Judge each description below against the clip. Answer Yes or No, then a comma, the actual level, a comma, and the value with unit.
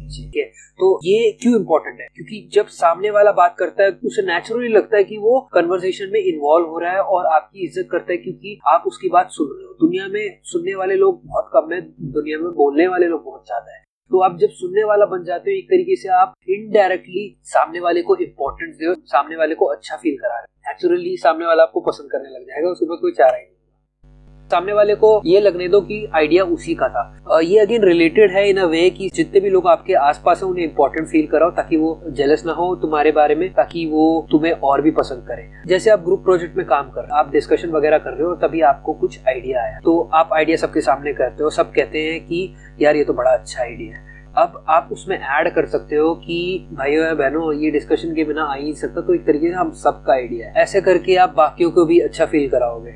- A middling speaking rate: No, fast, 245 wpm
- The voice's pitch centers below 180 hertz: No, high, 190 Hz